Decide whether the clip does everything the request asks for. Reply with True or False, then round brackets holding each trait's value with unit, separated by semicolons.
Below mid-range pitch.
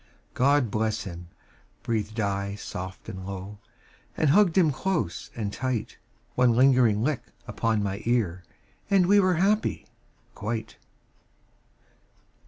True (115 Hz)